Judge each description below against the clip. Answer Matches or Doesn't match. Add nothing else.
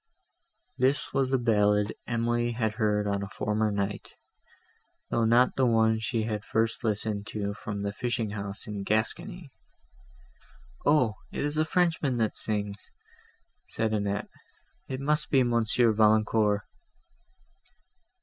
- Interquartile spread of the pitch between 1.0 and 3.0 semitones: Matches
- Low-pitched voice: Matches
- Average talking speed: Doesn't match